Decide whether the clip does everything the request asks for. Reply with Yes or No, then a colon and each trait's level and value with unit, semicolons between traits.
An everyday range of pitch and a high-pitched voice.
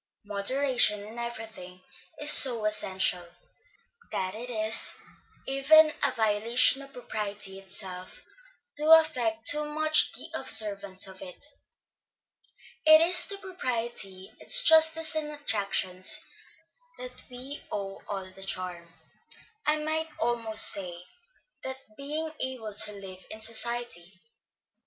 No: wide, 7.1 semitones; high, 230 Hz